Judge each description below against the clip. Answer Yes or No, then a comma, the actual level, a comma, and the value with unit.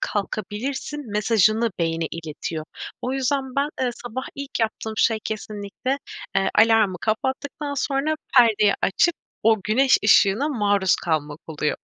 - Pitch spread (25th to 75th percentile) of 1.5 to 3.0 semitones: No, average, 4.9 semitones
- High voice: Yes, high, 220 Hz